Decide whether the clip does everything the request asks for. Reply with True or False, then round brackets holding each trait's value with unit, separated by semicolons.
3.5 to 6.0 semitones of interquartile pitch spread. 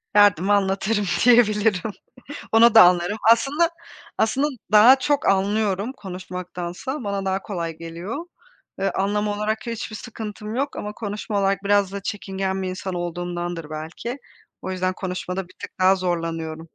False (3.0 semitones)